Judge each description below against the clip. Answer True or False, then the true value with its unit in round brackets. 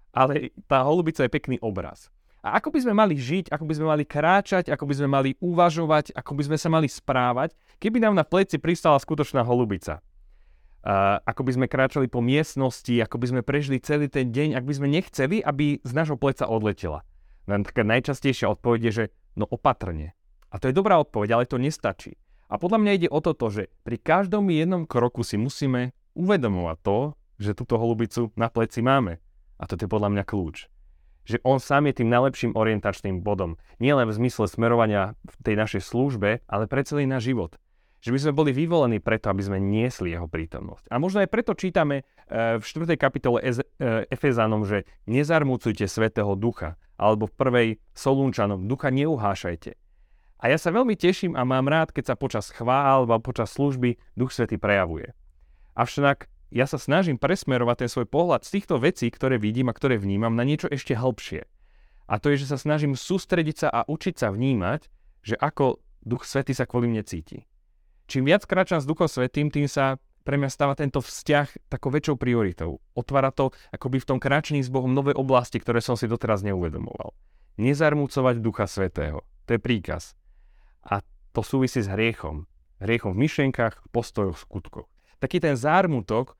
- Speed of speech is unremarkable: False (180 wpm)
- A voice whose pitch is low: True (125 Hz)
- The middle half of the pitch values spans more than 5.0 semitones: True (5.4 semitones)